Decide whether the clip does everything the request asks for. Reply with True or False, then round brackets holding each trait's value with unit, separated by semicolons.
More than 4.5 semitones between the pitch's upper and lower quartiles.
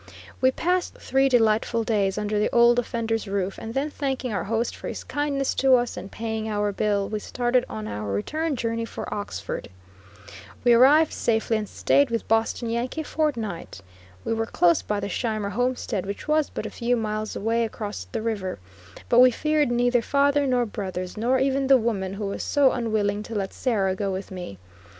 False (3.8 semitones)